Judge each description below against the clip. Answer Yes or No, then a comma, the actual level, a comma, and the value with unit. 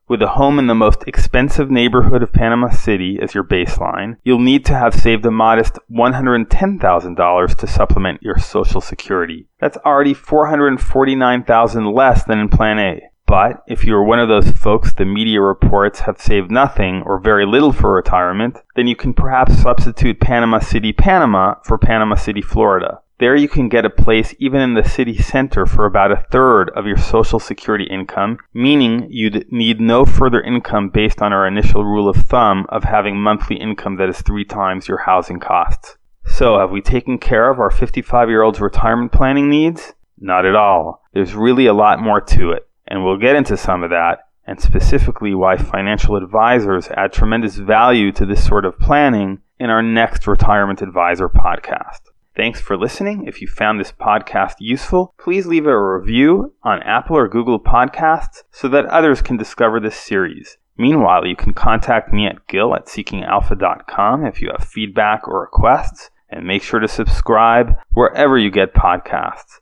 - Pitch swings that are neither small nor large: Yes, average, 3.5 semitones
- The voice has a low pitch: Yes, low, 110 Hz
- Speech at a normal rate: Yes, average, 185 wpm